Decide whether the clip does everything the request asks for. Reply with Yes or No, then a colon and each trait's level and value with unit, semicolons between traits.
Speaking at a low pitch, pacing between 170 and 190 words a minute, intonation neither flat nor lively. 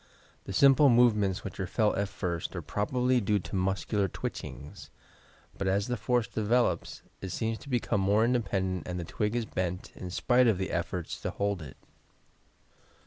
Yes: low, 100 Hz; average, 175 wpm; average, 4.3 semitones